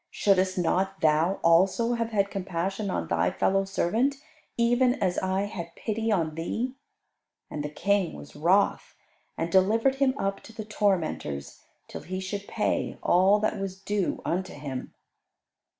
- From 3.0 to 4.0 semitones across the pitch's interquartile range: Yes, average, 3.5 semitones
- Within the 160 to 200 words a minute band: No, average, 150 wpm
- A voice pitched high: Yes, high, 195 Hz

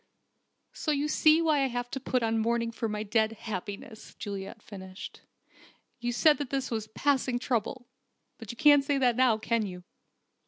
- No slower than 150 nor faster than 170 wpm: No, average, 180 wpm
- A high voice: Yes, high, 235 Hz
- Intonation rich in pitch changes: No, average, 3.7 semitones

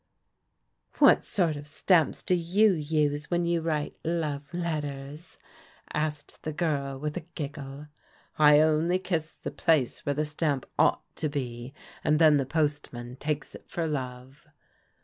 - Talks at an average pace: Yes, average, 165 wpm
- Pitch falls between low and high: Yes, medium, 150 Hz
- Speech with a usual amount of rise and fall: No, narrow, 2.3 semitones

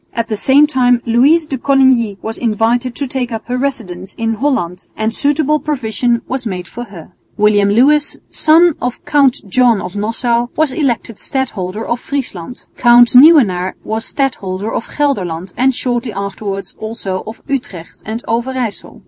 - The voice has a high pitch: Yes, high, 235 Hz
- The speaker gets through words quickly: No, average, 155 wpm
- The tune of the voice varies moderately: Yes, average, 4.1 semitones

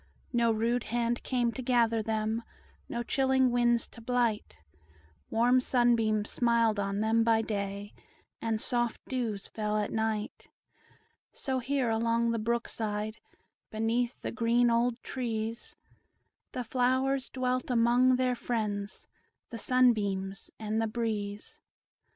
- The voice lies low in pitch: No, high, 230 Hz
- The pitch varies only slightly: Yes, narrow, 2.0 semitones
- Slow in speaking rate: Yes, slow, 125 wpm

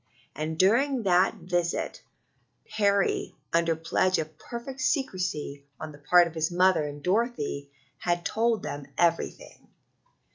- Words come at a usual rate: No, slow, 130 wpm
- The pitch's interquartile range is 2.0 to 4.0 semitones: No, average, 4.6 semitones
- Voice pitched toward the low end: No, medium, 175 Hz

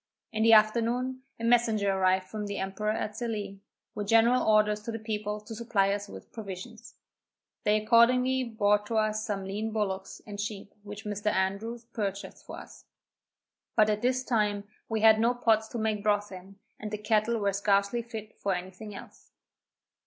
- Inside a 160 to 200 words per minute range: Yes, average, 175 wpm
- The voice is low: No, high, 215 Hz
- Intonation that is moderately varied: No, narrow, 1.9 semitones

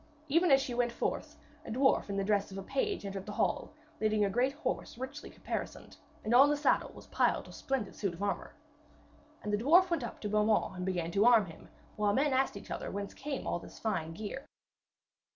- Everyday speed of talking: No, fast, 220 wpm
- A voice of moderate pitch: No, high, 220 Hz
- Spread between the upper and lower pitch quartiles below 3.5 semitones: No, average, 5.2 semitones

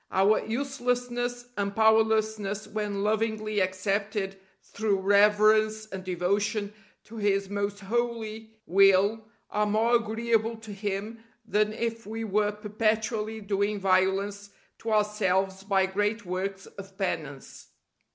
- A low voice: No, high, 210 Hz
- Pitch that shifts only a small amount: Yes, narrow, 1.9 semitones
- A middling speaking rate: No, slow, 115 wpm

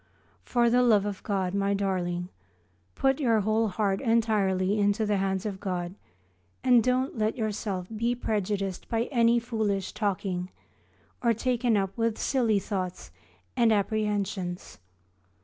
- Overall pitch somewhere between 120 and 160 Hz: No, high, 210 Hz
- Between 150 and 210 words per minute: No, slow, 135 wpm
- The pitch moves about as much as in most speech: Yes, average, 3.1 semitones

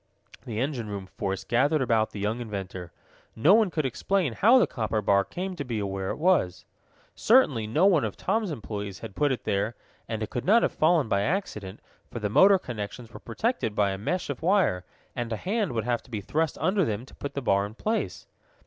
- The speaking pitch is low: Yes, low, 120 Hz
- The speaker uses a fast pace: Yes, fast, 220 wpm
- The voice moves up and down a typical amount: No, wide, 8.8 semitones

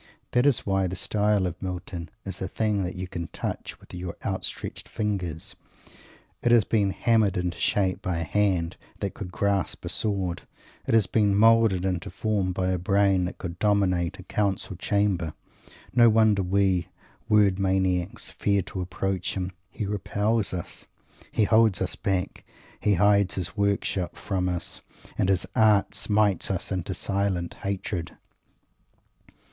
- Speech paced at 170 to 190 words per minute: No, average, 160 wpm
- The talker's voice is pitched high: No, very low, 95 Hz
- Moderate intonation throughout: No, narrow, 2.2 semitones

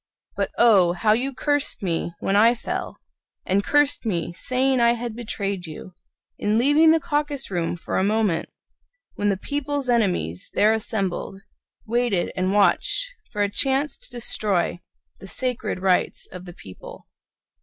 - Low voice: No, high, 215 Hz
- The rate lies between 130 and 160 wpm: Yes, average, 155 wpm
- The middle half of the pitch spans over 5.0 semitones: Yes, wide, 5.5 semitones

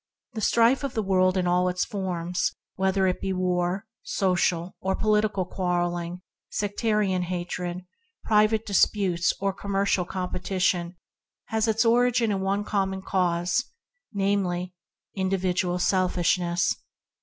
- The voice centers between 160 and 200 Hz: Yes, high, 190 Hz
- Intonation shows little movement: Yes, narrow, 2.2 semitones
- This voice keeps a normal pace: No, slow, 120 wpm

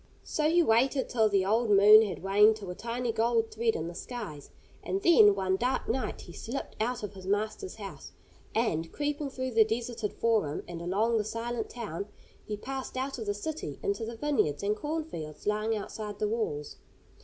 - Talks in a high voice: Yes, high, 220 Hz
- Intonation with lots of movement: No, average, 3.4 semitones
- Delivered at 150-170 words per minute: No, average, 195 wpm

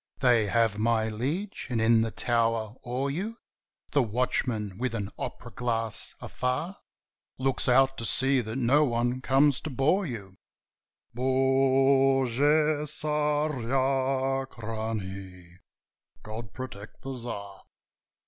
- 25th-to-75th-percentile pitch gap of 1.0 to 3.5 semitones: Yes, average, 3.2 semitones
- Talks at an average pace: No, slow, 110 wpm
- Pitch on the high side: No, low, 125 Hz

